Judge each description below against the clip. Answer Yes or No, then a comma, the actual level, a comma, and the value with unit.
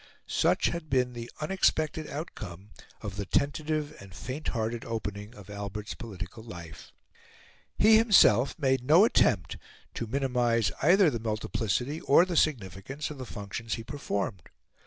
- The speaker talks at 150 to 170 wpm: No, slow, 135 wpm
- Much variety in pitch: Yes, wide, 6.6 semitones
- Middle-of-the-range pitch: No, low, 120 Hz